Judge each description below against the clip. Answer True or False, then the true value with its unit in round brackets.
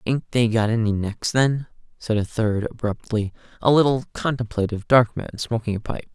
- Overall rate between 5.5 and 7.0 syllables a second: False (5.1 syllables/s)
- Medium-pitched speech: False (115 Hz)